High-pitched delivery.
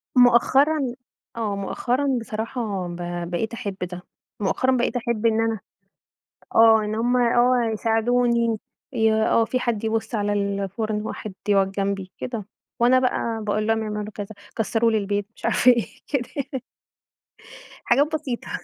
Yes: high, 225 Hz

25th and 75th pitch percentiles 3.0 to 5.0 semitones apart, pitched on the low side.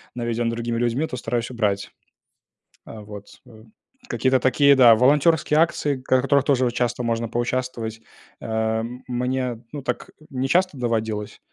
No: narrow, 2.5 semitones; low, 120 Hz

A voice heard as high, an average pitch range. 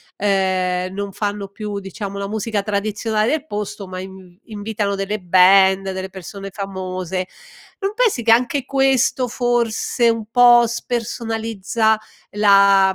Yes: high, 205 Hz; average, 3.0 semitones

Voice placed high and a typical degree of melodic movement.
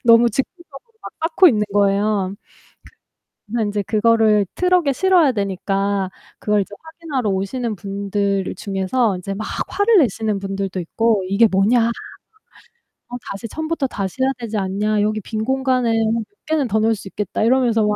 Yes: high, 220 Hz; average, 4.4 semitones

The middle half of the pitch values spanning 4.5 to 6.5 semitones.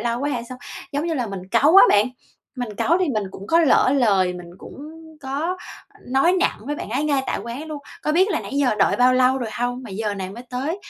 Yes: average, 4.8 semitones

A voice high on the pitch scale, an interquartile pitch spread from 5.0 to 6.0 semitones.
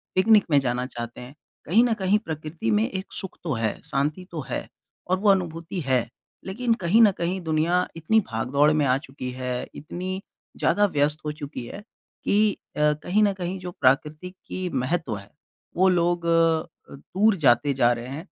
No: medium, 160 Hz; wide, 5.6 semitones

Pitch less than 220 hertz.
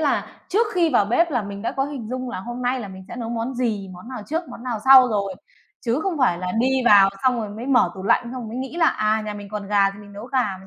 No: high, 235 Hz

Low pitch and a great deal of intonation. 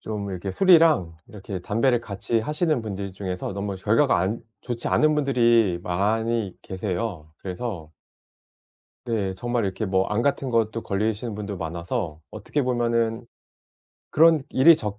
No: low, 110 Hz; average, 4.0 semitones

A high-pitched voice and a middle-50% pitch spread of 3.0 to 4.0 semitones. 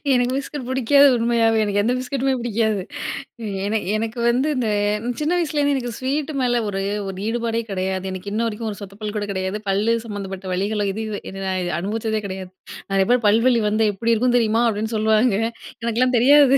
Yes: high, 225 Hz; average, 3.3 semitones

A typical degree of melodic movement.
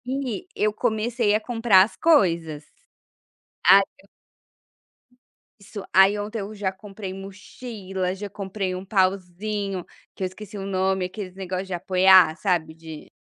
No: narrow, 2.2 semitones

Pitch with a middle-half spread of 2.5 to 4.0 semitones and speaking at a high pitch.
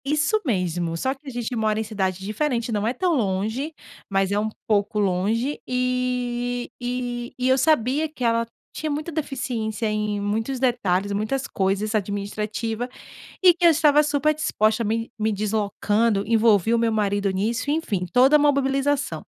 No: average, 4.4 semitones; high, 230 Hz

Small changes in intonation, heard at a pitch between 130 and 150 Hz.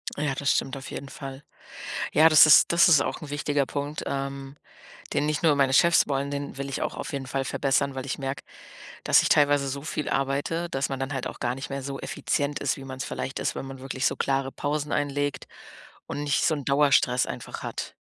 Yes: narrow, 1.3 semitones; medium, 140 Hz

